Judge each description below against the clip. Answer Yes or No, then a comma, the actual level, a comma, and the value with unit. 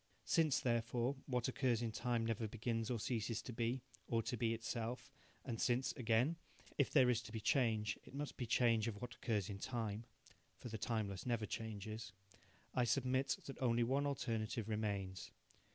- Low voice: Yes, low, 115 Hz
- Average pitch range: No, narrow, 2.2 semitones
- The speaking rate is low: No, average, 175 wpm